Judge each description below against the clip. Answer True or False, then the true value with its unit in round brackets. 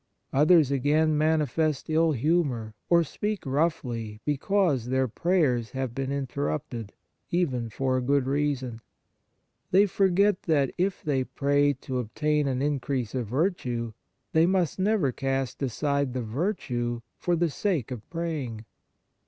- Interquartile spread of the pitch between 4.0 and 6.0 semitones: True (4.5 semitones)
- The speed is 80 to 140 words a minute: True (135 wpm)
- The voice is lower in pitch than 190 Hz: True (140 Hz)